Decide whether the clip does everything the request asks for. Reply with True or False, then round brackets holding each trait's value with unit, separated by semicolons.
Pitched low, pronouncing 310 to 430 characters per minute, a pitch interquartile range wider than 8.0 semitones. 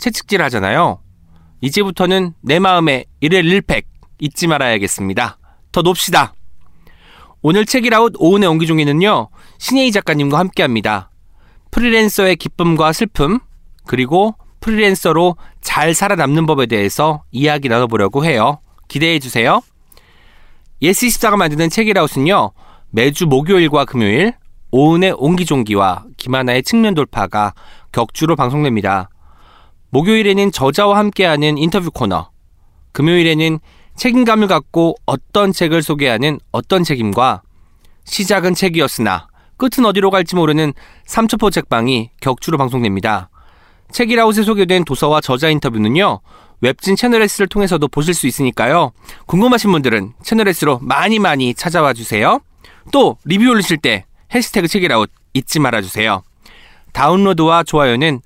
False (155 Hz; 320 characters per minute; 8.6 semitones)